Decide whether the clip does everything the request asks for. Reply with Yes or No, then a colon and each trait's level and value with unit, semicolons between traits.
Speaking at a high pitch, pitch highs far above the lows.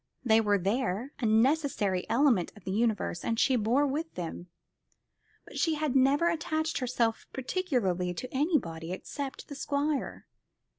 Yes: very high, 250 Hz; wide, 5.9 semitones